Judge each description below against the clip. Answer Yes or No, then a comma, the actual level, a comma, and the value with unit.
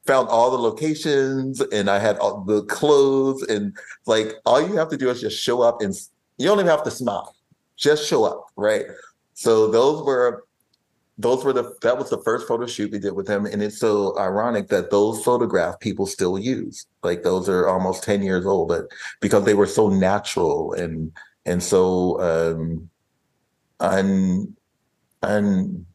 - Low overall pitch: Yes, low, 110 Hz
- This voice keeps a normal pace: Yes, average, 180 wpm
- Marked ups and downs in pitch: Yes, wide, 6.0 semitones